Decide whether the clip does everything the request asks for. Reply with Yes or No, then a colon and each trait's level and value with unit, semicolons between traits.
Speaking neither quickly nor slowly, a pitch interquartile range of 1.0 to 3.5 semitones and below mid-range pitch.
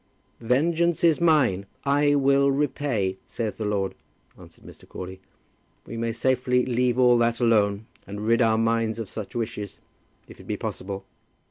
No: average, 155 wpm; average, 4.4 semitones; low, 115 Hz